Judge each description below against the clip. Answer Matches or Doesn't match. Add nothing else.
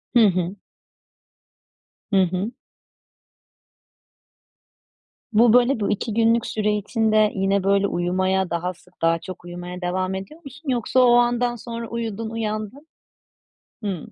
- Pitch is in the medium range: Doesn't match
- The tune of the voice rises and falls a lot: Doesn't match